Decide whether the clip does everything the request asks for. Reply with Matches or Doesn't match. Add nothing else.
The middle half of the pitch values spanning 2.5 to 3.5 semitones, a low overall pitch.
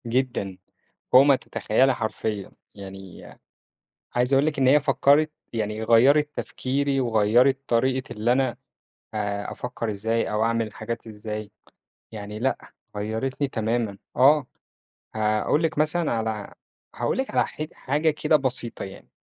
Doesn't match